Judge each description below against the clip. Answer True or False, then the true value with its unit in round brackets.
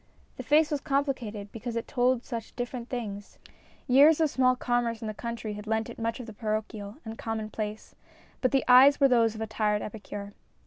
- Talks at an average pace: False (210 wpm)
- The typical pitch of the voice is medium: False (230 Hz)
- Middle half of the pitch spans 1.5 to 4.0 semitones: True (2.9 semitones)